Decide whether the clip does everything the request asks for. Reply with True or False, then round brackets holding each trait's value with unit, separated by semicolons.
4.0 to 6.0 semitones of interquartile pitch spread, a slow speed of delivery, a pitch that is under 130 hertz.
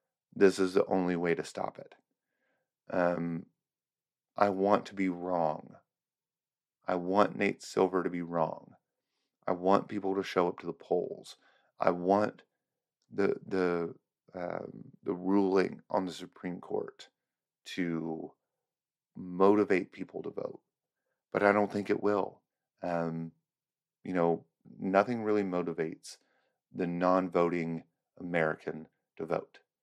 False (2.5 semitones; 125 wpm; 90 Hz)